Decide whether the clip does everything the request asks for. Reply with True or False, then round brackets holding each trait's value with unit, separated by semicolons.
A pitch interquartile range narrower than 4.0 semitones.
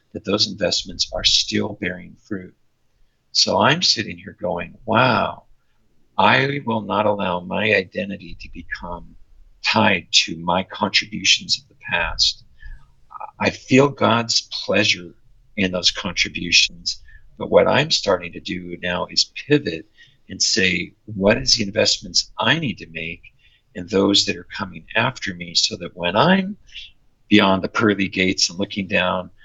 True (3.4 semitones)